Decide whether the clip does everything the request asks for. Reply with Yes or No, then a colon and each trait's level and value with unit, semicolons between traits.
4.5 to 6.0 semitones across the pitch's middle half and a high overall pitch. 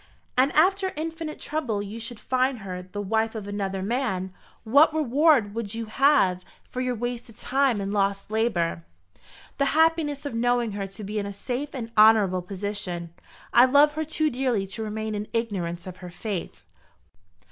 Yes: average, 5.3 semitones; high, 225 Hz